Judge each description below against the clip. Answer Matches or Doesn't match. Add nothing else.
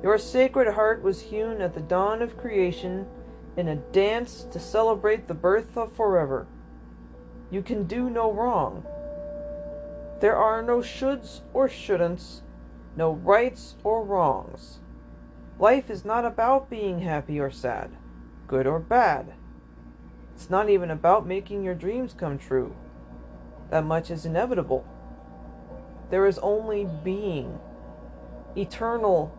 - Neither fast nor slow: Doesn't match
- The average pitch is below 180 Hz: Doesn't match